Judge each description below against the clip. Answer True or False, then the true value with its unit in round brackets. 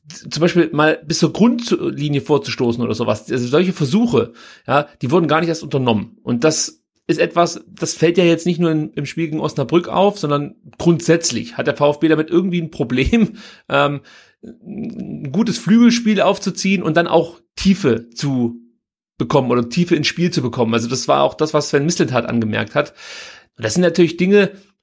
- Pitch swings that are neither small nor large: True (4.2 semitones)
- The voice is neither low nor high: True (160 Hz)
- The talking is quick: False (180 wpm)